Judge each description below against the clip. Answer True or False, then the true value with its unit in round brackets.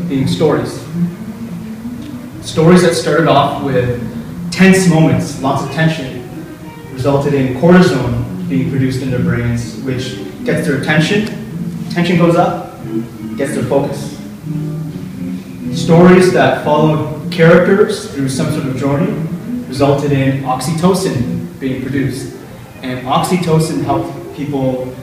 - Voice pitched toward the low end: False (155 Hz)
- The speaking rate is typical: False (115 wpm)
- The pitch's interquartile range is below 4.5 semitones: False (4.9 semitones)